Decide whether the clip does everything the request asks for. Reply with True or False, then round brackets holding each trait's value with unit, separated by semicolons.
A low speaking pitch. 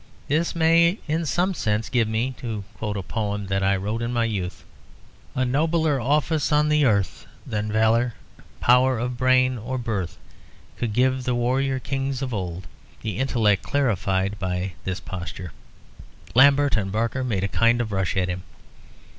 True (115 Hz)